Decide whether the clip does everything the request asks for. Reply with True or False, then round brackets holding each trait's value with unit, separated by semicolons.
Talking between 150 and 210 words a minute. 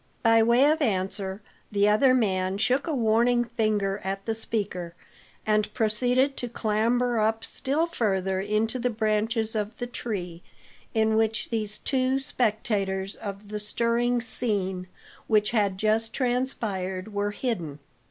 False (140 wpm)